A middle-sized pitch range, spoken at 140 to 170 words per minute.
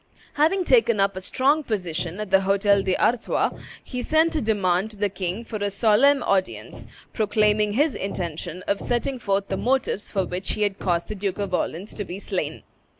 No: average, 3.6 semitones; average, 190 wpm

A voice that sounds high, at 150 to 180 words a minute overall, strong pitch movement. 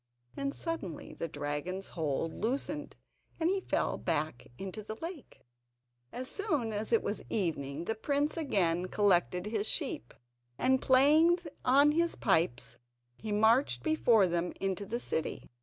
No: high, 215 Hz; average, 140 wpm; wide, 8.2 semitones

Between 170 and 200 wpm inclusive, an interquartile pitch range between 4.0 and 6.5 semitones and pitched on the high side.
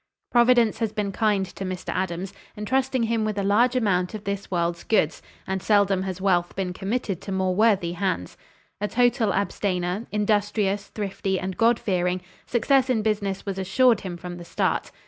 No: average, 175 wpm; average, 3.0 semitones; high, 200 Hz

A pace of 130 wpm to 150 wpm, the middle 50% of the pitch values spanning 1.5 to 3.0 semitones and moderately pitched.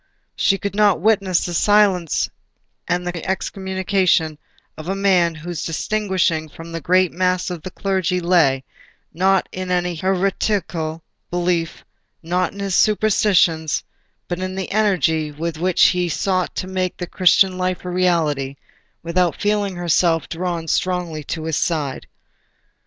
Yes: average, 140 wpm; narrow, 2.4 semitones; medium, 180 Hz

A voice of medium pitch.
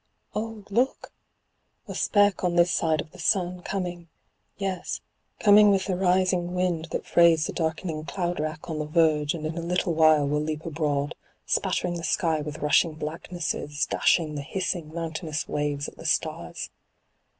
Yes: medium, 165 Hz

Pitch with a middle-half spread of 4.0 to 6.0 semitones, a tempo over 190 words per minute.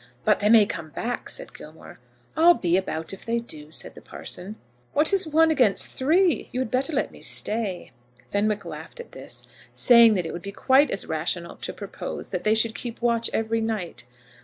Yes: average, 5.0 semitones; average, 200 wpm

